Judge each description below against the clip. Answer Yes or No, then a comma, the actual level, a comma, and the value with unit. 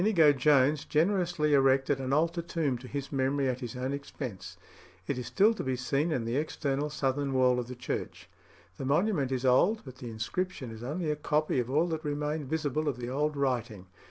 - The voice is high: No, medium, 140 Hz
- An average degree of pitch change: Yes, average, 3.1 semitones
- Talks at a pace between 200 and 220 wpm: Yes, fast, 205 wpm